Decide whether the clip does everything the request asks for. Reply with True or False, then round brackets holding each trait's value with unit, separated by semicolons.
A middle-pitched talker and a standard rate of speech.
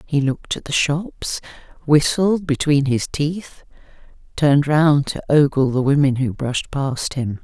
True (145 Hz; 155 wpm)